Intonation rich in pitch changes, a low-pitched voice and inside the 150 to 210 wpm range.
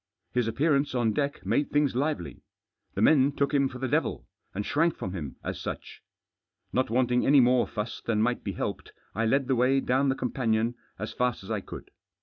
No: average, 3.4 semitones; low, 125 Hz; average, 200 wpm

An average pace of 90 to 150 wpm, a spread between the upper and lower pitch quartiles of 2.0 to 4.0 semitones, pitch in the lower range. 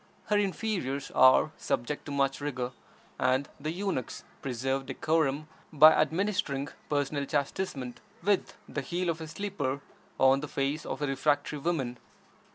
No: average, 140 wpm; average, 3.2 semitones; medium, 145 Hz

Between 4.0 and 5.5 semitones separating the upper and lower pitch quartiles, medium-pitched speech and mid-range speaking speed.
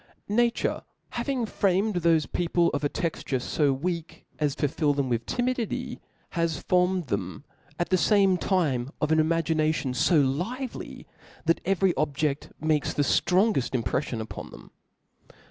Yes: average, 4.7 semitones; medium, 165 Hz; average, 145 wpm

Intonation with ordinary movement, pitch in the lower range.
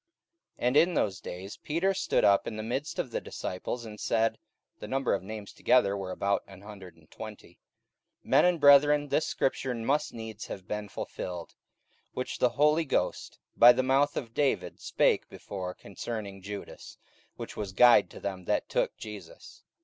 No: wide, 6.0 semitones; low, 115 Hz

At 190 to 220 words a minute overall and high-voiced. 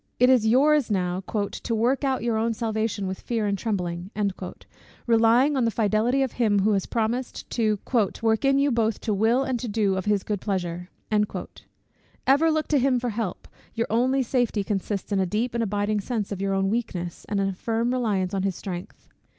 Yes: average, 200 wpm; high, 220 Hz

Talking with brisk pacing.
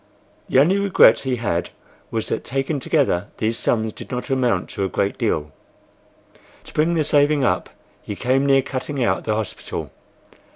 No: average, 170 wpm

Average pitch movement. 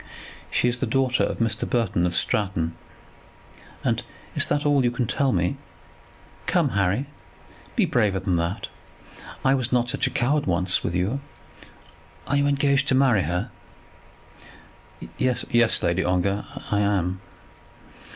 No: wide, 5.9 semitones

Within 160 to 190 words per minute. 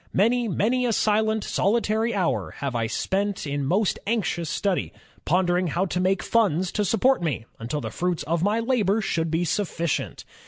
Yes: average, 180 wpm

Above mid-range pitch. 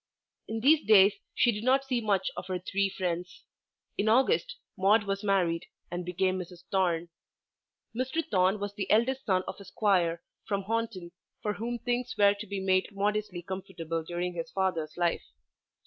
Yes: high, 195 Hz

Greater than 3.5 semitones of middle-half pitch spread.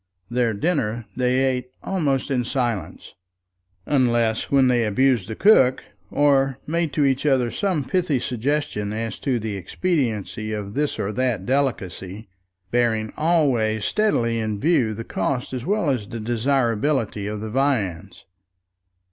Yes: average, 4.2 semitones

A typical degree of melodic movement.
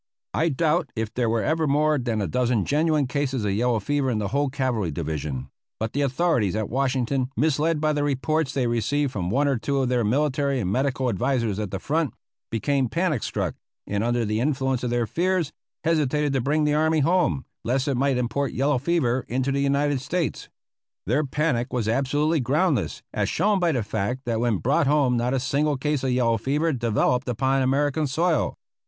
Yes: average, 3.7 semitones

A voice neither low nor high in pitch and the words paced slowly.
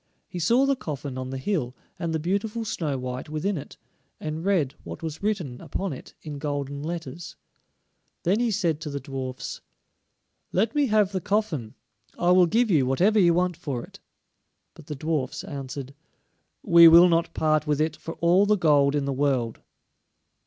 No: medium, 160 Hz; average, 180 wpm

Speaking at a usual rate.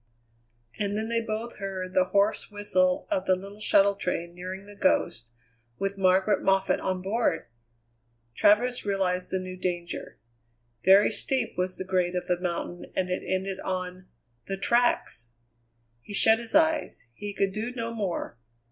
Yes: average, 155 wpm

